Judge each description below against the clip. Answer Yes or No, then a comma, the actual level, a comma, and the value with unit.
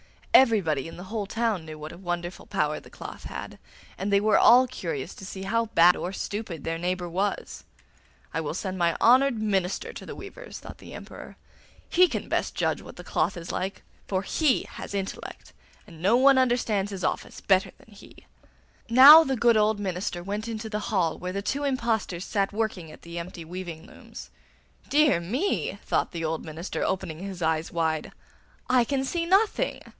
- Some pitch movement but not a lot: Yes, average, 5.0 semitones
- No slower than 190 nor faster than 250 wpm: Yes, average, 195 wpm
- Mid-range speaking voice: No, high, 195 Hz